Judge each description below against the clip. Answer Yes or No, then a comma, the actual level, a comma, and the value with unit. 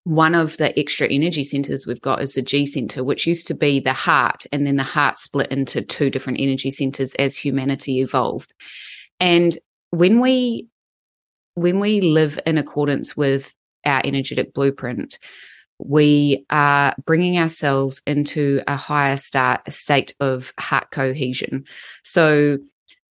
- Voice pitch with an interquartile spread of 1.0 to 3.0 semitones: Yes, narrow, 2.6 semitones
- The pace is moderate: Yes, average, 150 wpm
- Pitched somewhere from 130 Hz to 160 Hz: Yes, medium, 140 Hz